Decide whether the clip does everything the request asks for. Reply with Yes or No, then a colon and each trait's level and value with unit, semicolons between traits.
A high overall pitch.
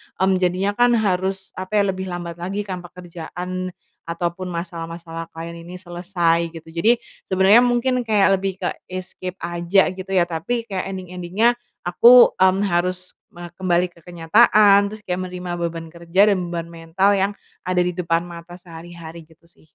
No: medium, 180 Hz